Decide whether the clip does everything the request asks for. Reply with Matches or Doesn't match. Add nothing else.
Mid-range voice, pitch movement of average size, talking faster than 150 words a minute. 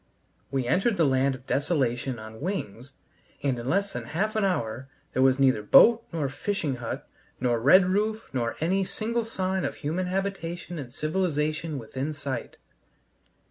Doesn't match